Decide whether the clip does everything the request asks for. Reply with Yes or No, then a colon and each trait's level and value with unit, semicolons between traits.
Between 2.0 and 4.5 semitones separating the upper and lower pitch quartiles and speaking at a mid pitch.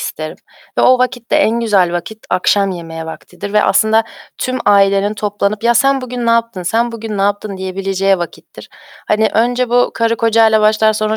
No: average, 2.8 semitones; high, 215 Hz